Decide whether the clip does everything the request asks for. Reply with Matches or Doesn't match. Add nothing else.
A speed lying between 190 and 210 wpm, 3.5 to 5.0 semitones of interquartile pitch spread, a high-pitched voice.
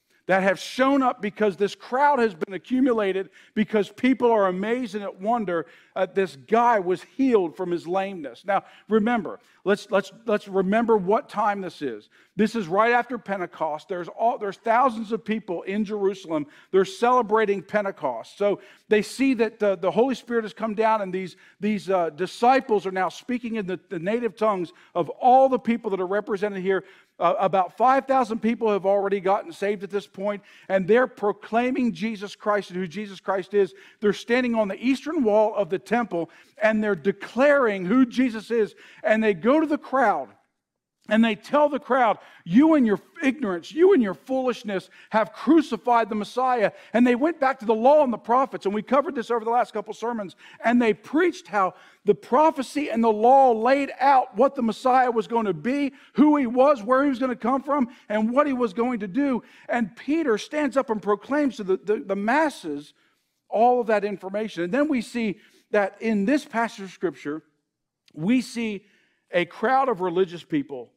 Matches